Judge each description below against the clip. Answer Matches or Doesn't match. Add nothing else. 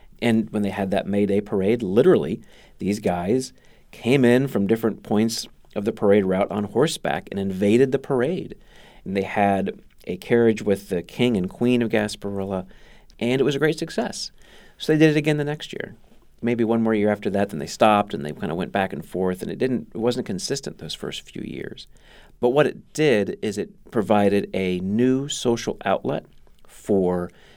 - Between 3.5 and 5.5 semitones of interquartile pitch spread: Matches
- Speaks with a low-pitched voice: Matches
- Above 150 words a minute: Matches